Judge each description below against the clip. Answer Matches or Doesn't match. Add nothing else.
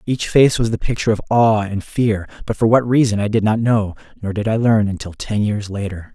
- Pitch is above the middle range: Doesn't match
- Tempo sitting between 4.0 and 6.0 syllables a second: Matches